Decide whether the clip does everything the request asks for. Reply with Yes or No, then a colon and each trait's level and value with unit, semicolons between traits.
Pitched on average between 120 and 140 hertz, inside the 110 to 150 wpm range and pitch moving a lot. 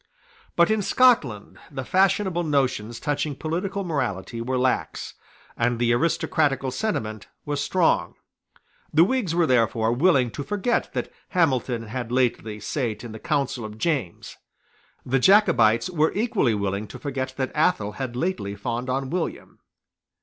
Yes: low, 135 Hz; average, 140 wpm; wide, 6.4 semitones